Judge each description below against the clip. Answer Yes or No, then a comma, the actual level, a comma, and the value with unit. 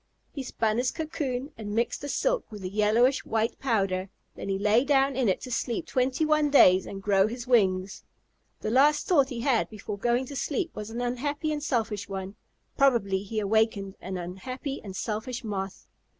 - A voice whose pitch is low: No, high, 230 Hz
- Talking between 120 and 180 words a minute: No, average, 190 wpm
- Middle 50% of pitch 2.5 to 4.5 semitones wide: No, average, 4.9 semitones